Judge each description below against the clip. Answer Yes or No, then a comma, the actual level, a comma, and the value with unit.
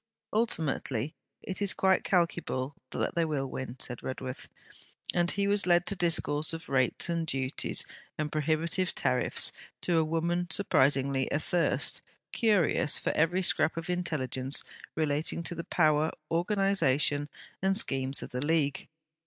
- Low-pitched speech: No, medium, 160 Hz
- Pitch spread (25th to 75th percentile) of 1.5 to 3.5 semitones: No, average, 4.1 semitones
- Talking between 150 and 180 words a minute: No, average, 140 wpm